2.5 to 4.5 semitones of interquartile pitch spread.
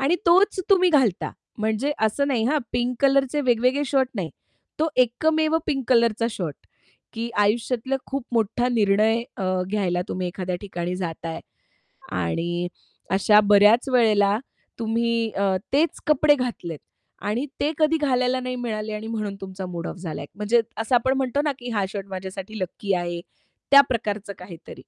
No: average, 5.0 semitones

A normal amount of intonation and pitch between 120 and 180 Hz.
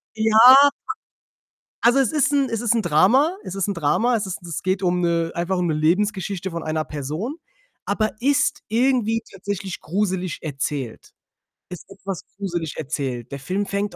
No: average, 4.9 semitones; high, 190 Hz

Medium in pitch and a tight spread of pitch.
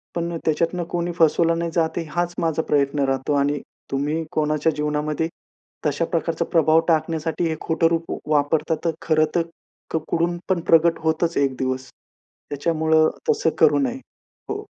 Yes: medium, 160 Hz; narrow, 2.1 semitones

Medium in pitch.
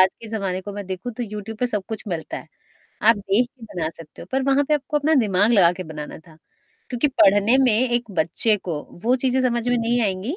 No: high, 215 Hz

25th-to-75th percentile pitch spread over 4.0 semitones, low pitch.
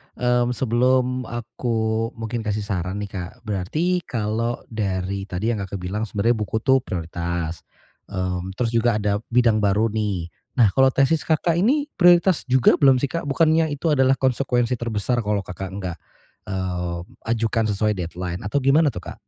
Yes: average, 4.8 semitones; low, 115 Hz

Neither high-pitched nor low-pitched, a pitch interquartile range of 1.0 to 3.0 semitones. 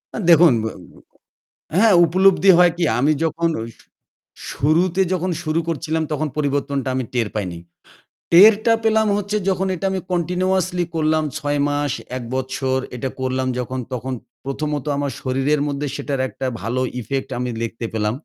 No: medium, 150 Hz; average, 5.2 semitones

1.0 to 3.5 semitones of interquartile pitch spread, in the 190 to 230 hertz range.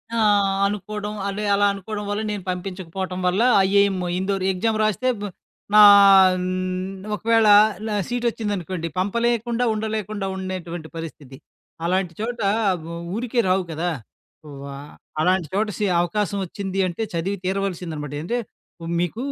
Yes: average, 2.9 semitones; high, 195 Hz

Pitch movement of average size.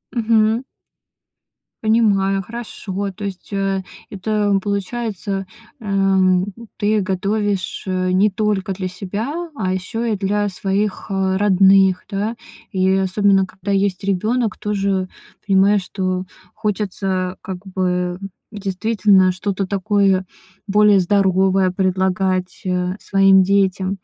No: narrow, 1.7 semitones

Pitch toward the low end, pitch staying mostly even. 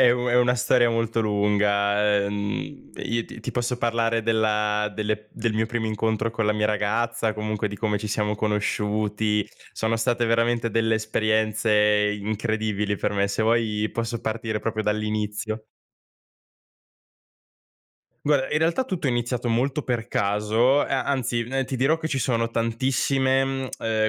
Yes: low, 110 Hz; narrow, 1.9 semitones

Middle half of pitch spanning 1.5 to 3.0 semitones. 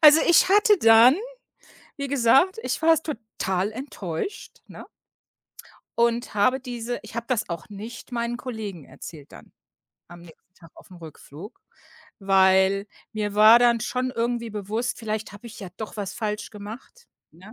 No: average, 3.8 semitones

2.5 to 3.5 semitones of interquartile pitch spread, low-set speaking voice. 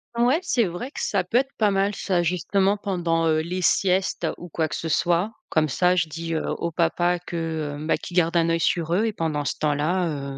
No: average, 2.9 semitones; medium, 175 Hz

